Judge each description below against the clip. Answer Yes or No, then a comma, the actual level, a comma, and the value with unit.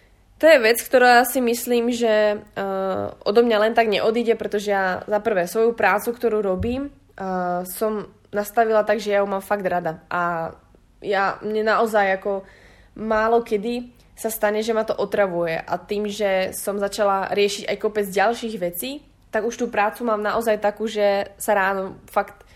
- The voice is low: No, high, 210 Hz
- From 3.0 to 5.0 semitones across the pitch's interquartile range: No, narrow, 2.4 semitones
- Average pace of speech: No, fast, 175 wpm